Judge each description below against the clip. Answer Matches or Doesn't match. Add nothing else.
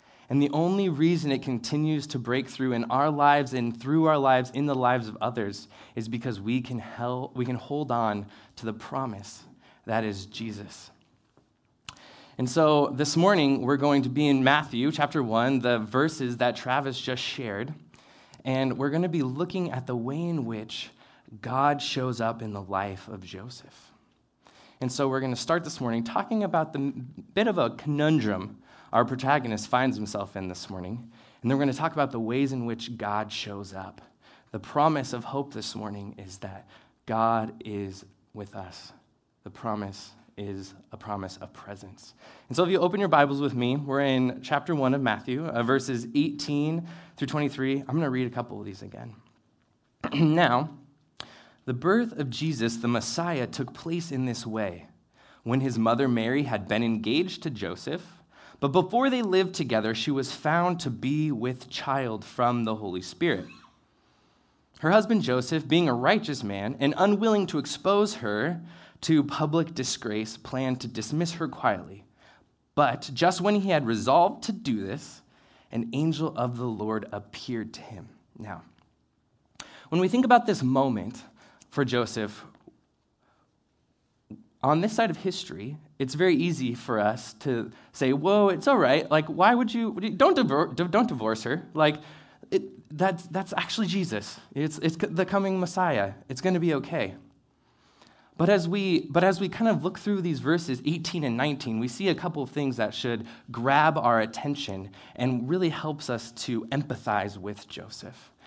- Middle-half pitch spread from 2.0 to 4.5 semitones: Doesn't match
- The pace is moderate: Matches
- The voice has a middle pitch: Doesn't match